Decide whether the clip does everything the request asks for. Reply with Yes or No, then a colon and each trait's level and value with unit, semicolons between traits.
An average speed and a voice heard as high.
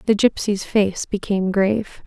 Yes: average, 145 wpm; high, 200 Hz